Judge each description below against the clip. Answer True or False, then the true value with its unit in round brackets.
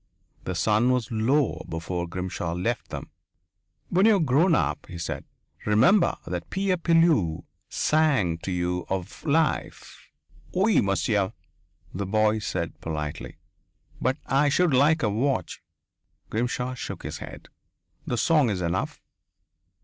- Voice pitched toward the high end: False (110 Hz)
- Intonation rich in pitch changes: True (8.8 semitones)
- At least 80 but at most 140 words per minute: True (135 wpm)